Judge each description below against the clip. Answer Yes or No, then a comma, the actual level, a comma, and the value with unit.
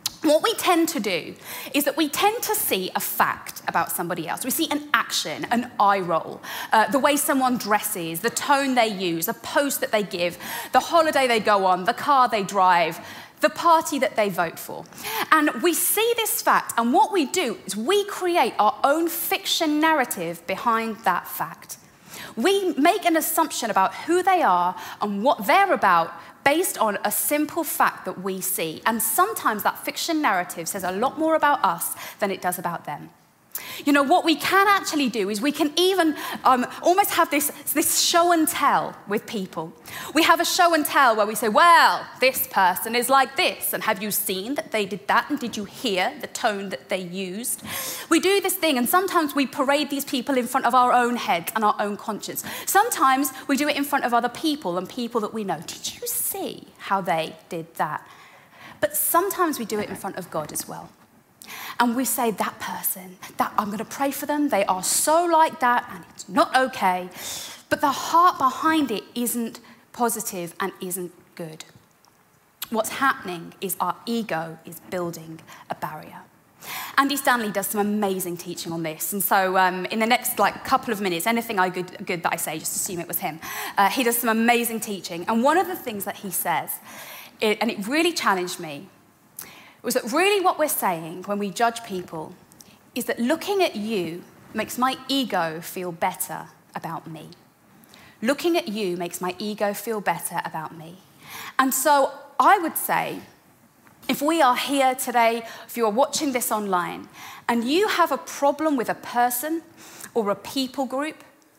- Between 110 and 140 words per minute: No, average, 195 wpm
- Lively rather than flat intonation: Yes, wide, 7.8 semitones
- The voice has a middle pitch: No, high, 240 Hz